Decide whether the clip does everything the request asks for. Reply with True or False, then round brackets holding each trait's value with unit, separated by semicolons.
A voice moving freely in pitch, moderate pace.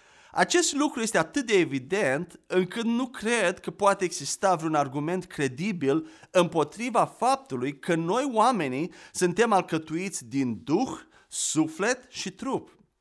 True (6.8 semitones; 125 wpm)